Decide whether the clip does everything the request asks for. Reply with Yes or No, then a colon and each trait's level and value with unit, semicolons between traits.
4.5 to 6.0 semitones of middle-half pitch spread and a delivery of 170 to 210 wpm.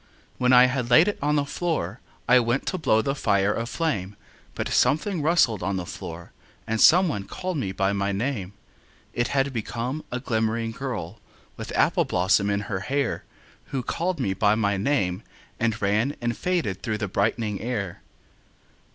Yes: wide, 5.4 semitones; average, 175 wpm